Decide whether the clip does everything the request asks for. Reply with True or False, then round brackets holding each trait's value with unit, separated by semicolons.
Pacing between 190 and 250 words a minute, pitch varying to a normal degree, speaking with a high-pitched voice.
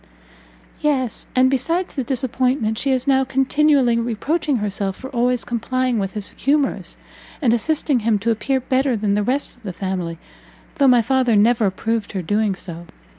False (170 wpm; 4.0 semitones; 245 Hz)